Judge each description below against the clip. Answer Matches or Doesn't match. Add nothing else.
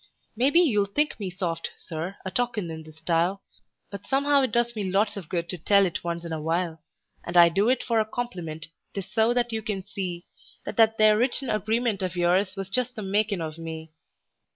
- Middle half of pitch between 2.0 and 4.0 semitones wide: Doesn't match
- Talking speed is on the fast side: Matches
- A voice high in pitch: Matches